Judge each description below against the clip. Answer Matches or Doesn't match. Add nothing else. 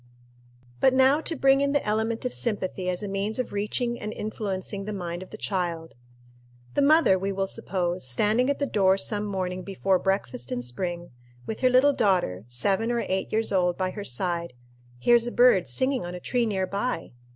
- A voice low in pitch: Doesn't match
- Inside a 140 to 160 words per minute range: Doesn't match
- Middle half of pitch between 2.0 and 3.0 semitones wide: Doesn't match